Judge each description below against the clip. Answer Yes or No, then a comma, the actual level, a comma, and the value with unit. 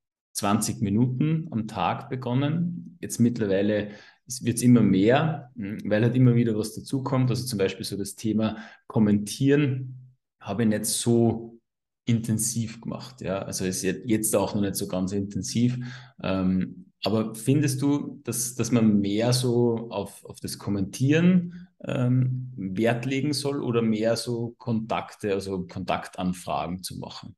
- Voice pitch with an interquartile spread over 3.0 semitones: Yes, average, 3.7 semitones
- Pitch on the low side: Yes, low, 115 Hz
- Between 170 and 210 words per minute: No, average, 140 wpm